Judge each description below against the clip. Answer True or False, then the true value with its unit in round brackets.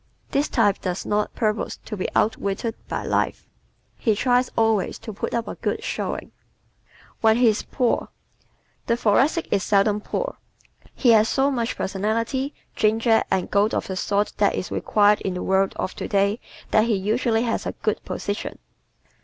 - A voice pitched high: True (215 Hz)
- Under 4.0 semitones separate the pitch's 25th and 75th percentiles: True (2.5 semitones)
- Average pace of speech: True (170 wpm)